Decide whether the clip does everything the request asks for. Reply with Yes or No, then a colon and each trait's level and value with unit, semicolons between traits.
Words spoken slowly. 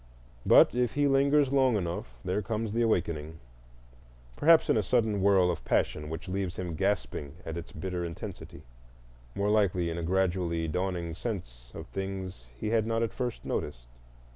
No: average, 165 wpm